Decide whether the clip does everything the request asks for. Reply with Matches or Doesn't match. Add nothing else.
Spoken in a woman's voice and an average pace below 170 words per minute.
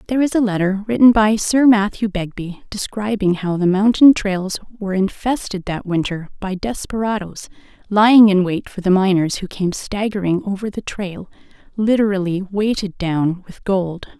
Matches